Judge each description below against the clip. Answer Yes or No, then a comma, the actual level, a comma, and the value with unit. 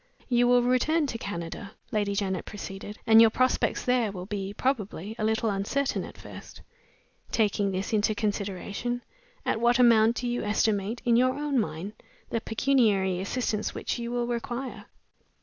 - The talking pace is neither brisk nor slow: Yes, average, 160 wpm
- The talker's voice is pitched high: Yes, high, 220 Hz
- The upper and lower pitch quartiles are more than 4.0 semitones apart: No, average, 3.2 semitones